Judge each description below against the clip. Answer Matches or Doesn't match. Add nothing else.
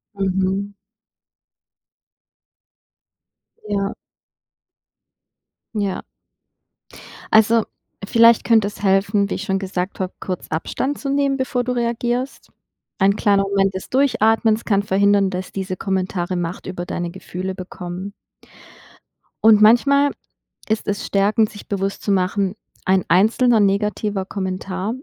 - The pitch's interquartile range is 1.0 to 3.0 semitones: Matches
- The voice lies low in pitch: Doesn't match